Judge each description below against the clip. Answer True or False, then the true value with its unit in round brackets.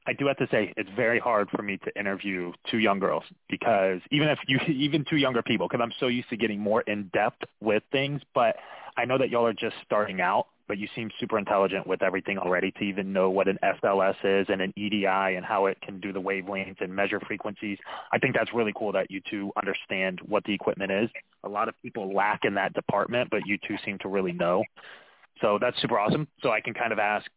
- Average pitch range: True (3.4 semitones)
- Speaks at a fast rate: True (240 wpm)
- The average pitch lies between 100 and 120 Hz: True (105 Hz)